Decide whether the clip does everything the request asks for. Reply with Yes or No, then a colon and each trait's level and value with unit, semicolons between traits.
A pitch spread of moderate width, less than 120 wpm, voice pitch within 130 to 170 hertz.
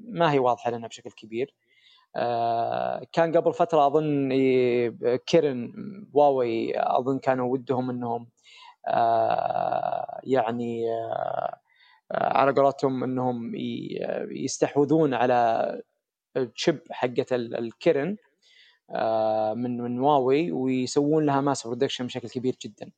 No: wide, 6.1 semitones; average, 90 wpm; low, 135 Hz